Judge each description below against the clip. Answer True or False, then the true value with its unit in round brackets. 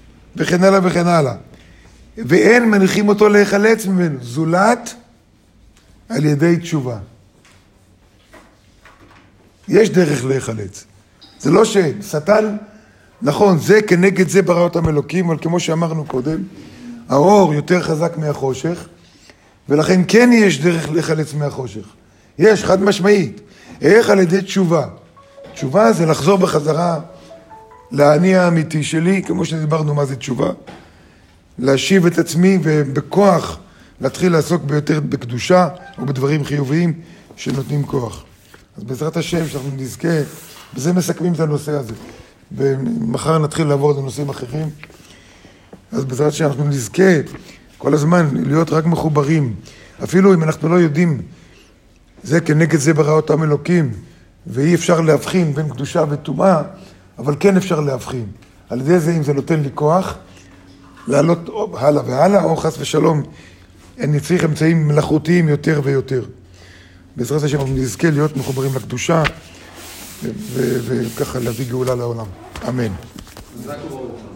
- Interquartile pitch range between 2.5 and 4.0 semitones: False (5.5 semitones)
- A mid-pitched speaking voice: True (150 Hz)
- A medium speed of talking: True (125 wpm)